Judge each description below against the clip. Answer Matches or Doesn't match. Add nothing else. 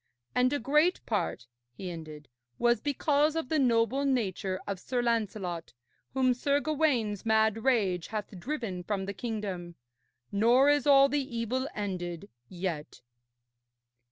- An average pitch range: Doesn't match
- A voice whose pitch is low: Doesn't match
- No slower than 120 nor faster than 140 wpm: Matches